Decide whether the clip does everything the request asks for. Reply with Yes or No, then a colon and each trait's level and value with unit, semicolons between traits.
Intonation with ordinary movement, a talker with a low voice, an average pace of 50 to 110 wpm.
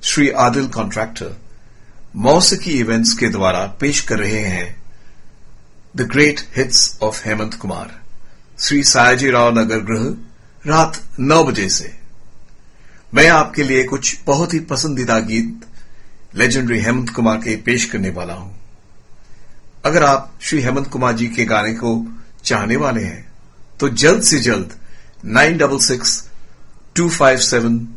No: average, 3.8 semitones; low, 120 Hz; average, 135 wpm